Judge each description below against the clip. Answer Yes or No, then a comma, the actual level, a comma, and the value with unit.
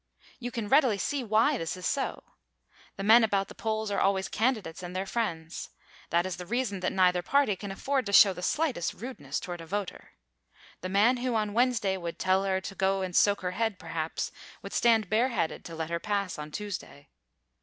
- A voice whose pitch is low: No, high, 200 Hz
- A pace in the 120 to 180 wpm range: No, fast, 205 wpm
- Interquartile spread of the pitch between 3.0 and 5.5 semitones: Yes, average, 3.9 semitones